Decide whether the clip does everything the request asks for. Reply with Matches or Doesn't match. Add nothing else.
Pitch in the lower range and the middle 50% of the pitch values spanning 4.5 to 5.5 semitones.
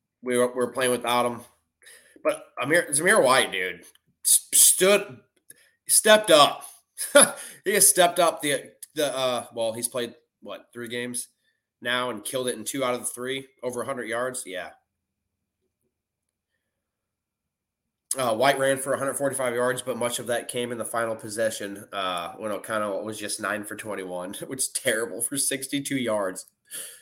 Doesn't match